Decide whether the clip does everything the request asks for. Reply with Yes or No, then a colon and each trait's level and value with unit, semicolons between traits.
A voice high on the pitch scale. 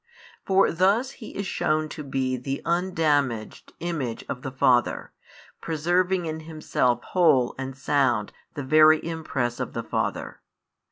No: medium, 155 Hz